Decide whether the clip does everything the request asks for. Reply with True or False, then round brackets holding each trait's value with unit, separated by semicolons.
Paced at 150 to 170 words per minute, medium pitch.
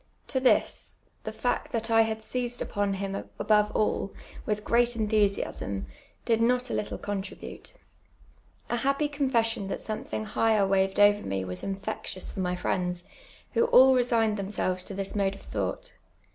False (160 wpm; 210 Hz)